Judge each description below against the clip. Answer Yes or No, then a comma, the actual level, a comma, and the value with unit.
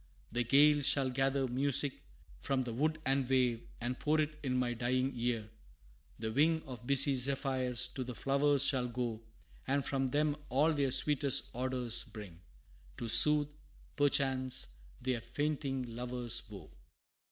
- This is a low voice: Yes, low, 130 Hz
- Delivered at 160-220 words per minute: No, average, 145 wpm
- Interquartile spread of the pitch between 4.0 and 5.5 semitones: No, narrow, 2.5 semitones